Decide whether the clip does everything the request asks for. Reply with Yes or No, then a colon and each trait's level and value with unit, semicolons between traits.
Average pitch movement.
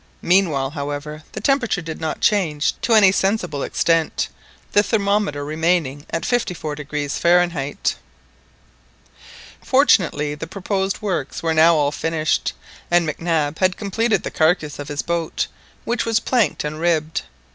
Yes: average, 4.7 semitones